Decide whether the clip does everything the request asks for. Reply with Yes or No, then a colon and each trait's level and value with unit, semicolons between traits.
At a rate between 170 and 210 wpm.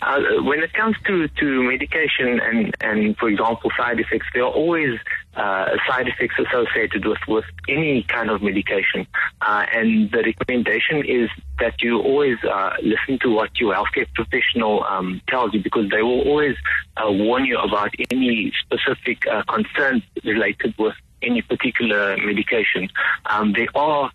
No: average, 160 wpm